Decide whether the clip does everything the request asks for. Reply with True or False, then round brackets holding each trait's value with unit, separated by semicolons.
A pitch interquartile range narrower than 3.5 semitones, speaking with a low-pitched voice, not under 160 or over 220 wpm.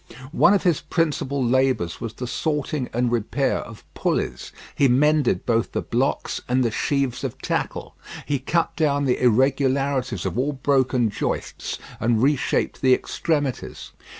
False (2.8 semitones; 130 Hz; 150 wpm)